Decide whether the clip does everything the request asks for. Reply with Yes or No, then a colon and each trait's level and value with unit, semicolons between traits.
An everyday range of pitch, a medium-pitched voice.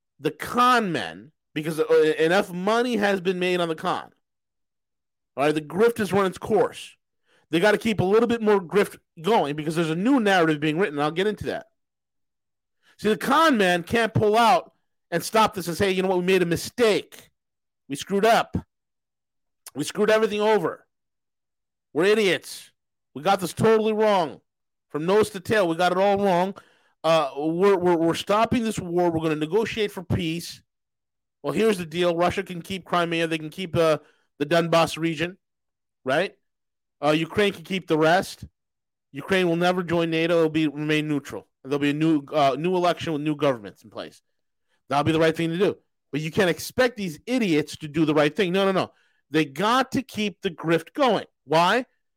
Yes: average, 4.4 semitones; medium, 175 Hz